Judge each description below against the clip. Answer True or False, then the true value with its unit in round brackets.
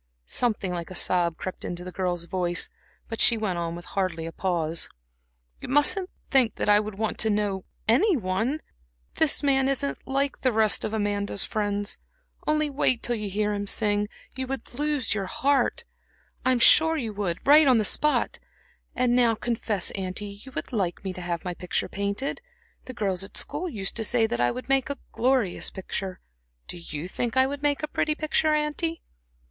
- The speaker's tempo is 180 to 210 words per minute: True (185 wpm)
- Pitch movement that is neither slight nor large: False (6.1 semitones)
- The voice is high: True (215 Hz)